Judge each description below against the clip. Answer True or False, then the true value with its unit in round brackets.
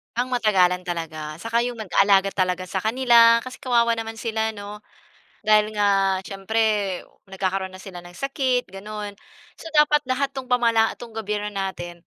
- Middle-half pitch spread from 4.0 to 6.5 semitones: False (3.4 semitones)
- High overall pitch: True (210 Hz)